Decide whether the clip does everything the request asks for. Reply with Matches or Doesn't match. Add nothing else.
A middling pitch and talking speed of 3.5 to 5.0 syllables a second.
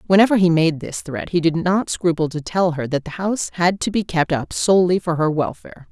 Doesn't match